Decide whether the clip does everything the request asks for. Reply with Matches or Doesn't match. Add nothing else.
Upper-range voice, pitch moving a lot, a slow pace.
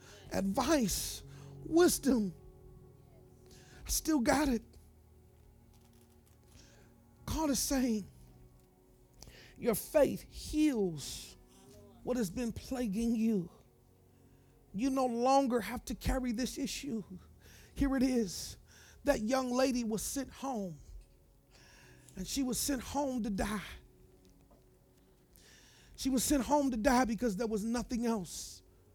Matches